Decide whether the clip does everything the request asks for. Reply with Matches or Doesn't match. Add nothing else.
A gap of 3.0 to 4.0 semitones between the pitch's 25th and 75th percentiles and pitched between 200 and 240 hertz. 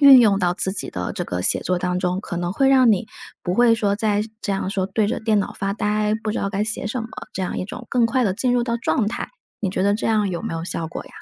Matches